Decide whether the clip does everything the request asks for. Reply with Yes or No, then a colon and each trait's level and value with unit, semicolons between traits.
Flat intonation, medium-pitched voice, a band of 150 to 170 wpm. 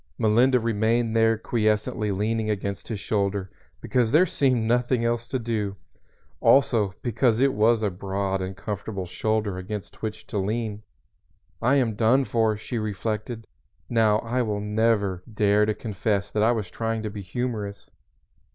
No: narrow, 2.2 semitones; low, 110 Hz; average, 155 wpm